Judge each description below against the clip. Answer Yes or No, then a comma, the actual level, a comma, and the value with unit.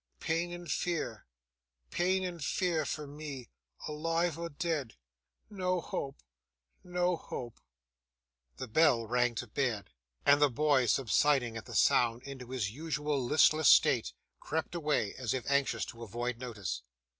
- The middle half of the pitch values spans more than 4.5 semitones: Yes, average, 5.2 semitones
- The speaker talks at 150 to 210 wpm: No, average, 140 wpm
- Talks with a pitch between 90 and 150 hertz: Yes, medium, 140 Hz